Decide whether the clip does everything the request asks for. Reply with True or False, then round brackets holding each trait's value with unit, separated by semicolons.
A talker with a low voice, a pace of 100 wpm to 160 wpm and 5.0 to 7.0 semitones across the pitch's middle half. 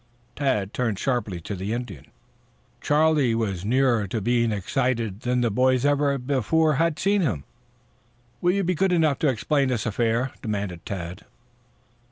True (125 Hz; 155 wpm; 5.4 semitones)